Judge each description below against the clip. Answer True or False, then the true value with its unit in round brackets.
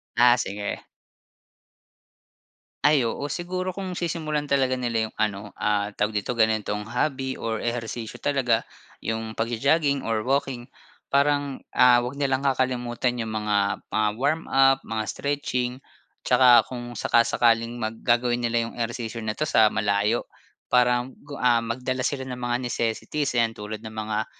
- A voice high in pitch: False (120 Hz)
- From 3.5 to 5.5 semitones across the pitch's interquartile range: False (3.1 semitones)